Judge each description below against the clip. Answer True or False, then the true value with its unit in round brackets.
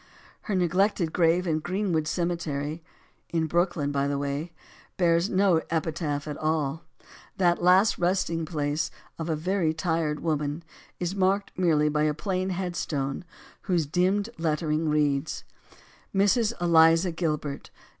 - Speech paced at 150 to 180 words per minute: False (135 wpm)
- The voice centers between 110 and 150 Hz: False (165 Hz)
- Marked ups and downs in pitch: False (3.0 semitones)